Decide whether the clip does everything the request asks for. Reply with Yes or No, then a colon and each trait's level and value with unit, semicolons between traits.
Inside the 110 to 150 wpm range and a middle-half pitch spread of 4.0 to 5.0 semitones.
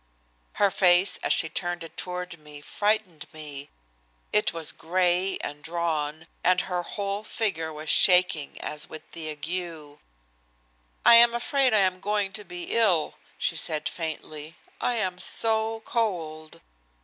Yes: average, 145 wpm; average, 4.3 semitones